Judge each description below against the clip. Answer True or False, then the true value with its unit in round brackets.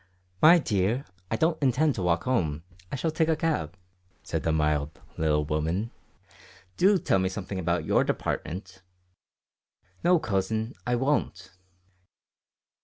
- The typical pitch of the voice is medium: False (100 Hz)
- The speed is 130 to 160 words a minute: True (135 wpm)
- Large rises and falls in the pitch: True (8.8 semitones)